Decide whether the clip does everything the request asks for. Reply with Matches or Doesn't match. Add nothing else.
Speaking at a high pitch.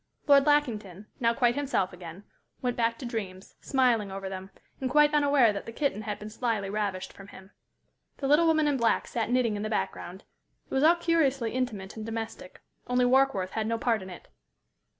Matches